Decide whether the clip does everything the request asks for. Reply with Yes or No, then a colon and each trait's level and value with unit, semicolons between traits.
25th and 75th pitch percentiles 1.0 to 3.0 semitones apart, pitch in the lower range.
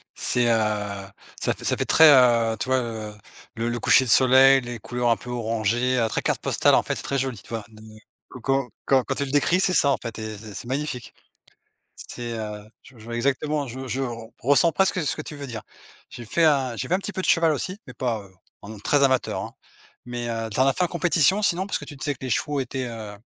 No: average, 3.7 semitones; low, 125 Hz